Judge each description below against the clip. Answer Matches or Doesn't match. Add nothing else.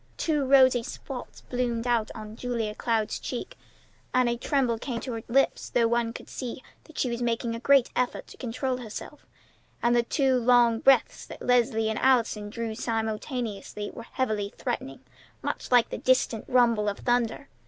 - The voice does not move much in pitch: Matches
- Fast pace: Doesn't match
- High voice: Matches